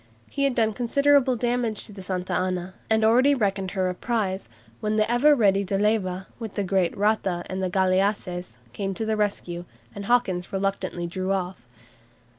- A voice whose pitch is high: Yes, high, 200 Hz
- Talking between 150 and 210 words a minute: Yes, average, 180 wpm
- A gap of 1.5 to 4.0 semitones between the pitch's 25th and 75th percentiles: Yes, average, 3.1 semitones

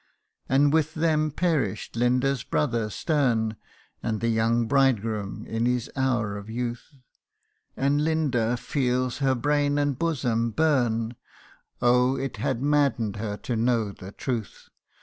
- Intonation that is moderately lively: Yes, average, 3.9 semitones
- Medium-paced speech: No, slow, 130 wpm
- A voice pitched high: No, low, 125 Hz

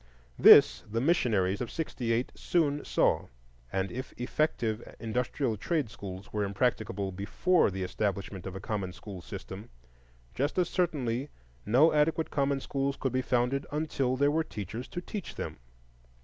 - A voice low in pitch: Yes, low, 125 Hz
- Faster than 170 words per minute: No, average, 150 wpm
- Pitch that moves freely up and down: Yes, wide, 6.1 semitones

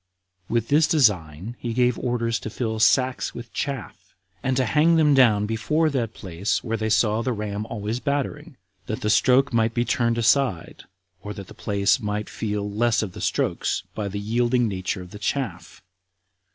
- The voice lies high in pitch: No, low, 115 Hz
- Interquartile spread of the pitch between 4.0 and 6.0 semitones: No, average, 3.5 semitones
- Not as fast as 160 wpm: No, average, 180 wpm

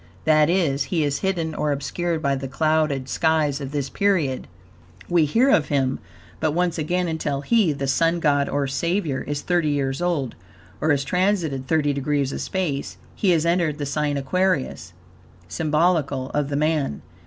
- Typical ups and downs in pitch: Yes, average, 3.4 semitones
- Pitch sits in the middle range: Yes, medium, 150 Hz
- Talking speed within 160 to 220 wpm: Yes, average, 170 wpm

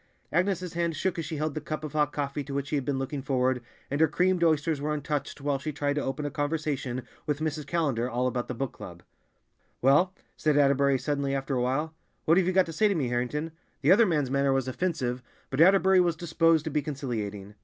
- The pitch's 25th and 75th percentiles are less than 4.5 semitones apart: Yes, average, 3.2 semitones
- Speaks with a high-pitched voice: No, medium, 145 Hz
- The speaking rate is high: Yes, fast, 230 wpm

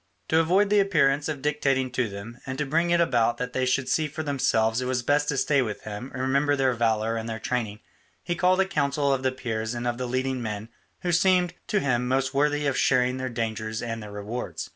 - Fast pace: Yes, fast, 235 wpm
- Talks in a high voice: No, low, 130 Hz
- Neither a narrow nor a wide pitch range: Yes, average, 3.9 semitones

